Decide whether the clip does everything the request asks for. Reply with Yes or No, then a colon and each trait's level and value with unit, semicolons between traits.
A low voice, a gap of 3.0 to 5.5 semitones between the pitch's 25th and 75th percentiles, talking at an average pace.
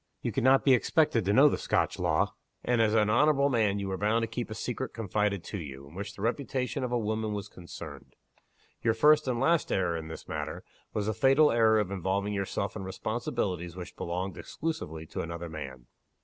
No: low, 105 Hz; average, 5.1 semitones; fast, 210 wpm